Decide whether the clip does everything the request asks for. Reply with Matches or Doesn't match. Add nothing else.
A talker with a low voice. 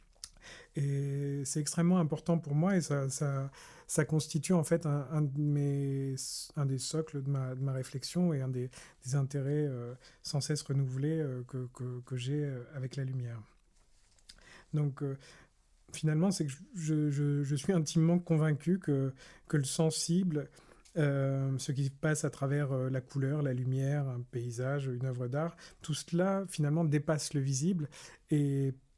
Doesn't match